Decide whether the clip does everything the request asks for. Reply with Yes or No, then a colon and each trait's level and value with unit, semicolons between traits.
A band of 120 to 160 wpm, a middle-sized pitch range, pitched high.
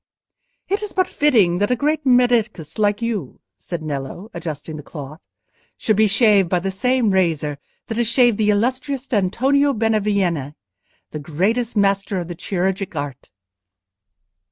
No: average, 150 wpm; wide, 5.8 semitones; high, 205 Hz